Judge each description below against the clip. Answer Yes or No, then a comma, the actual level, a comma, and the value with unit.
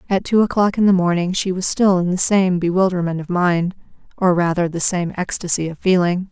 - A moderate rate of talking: No, fast, 210 wpm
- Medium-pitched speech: Yes, medium, 180 Hz